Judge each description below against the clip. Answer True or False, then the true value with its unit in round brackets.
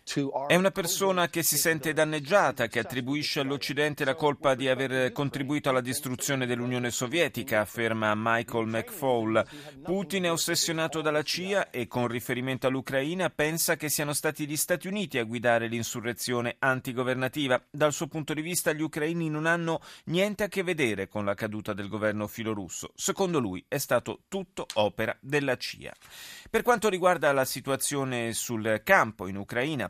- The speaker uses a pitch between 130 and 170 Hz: True (140 Hz)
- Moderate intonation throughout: True (5.0 semitones)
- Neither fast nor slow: True (155 wpm)